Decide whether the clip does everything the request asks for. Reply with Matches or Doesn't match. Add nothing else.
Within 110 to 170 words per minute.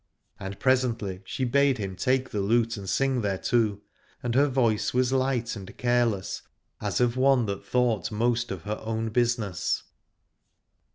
Matches